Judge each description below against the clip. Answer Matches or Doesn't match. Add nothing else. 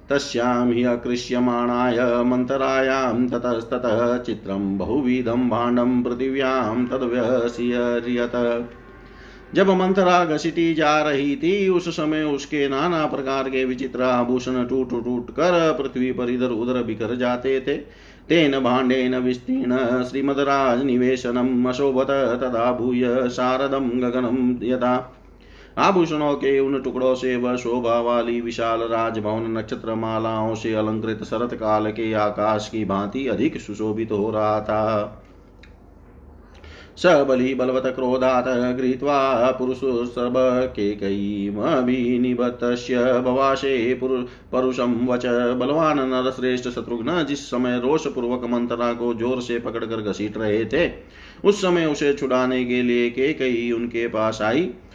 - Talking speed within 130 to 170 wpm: Doesn't match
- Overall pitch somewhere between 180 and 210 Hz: Doesn't match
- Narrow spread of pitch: Matches